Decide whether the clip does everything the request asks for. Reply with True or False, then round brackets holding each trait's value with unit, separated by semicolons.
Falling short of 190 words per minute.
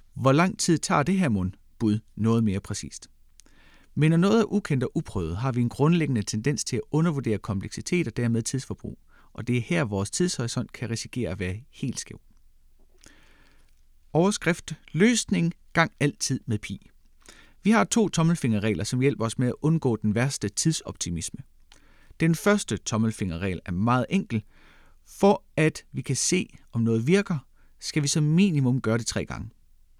True (165 wpm)